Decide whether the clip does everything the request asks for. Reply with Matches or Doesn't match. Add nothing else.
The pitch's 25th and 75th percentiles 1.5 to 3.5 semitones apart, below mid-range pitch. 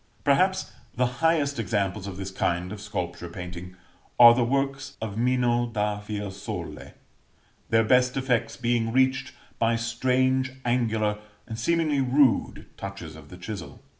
Doesn't match